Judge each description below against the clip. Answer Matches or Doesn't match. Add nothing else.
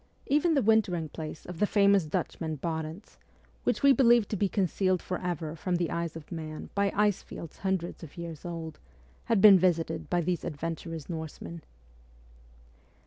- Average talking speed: Matches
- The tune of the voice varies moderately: Matches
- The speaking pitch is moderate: Matches